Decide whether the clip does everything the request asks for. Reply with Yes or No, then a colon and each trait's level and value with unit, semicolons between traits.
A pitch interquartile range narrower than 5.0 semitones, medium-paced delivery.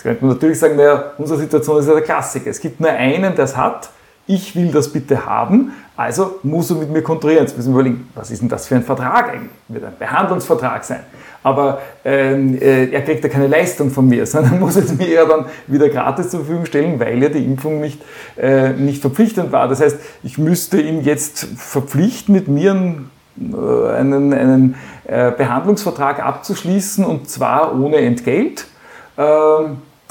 No: average, 3.4 semitones; fast, 195 wpm